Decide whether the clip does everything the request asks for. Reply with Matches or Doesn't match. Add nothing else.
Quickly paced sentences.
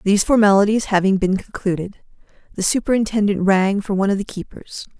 Doesn't match